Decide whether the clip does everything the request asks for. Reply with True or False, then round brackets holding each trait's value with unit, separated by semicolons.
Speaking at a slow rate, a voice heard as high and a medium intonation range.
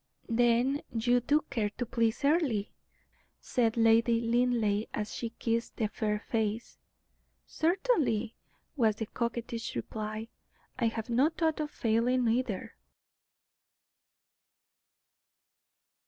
False (105 wpm; 230 Hz; 2.1 semitones)